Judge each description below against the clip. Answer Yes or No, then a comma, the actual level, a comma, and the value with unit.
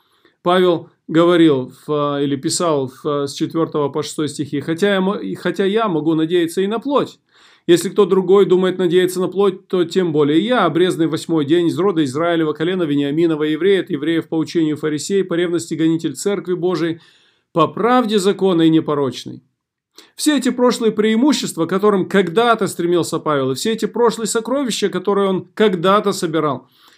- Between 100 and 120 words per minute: No, average, 150 wpm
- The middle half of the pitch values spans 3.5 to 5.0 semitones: Yes, average, 3.8 semitones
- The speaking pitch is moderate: Yes, medium, 175 Hz